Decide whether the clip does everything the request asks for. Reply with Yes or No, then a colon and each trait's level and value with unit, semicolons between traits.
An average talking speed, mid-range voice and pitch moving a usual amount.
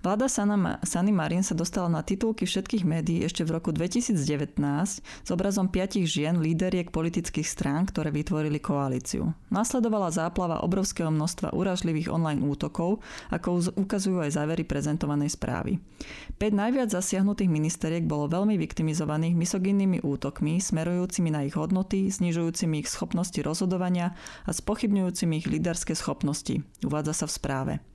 Yes: average, 135 wpm; medium, 175 Hz; average, 3.5 semitones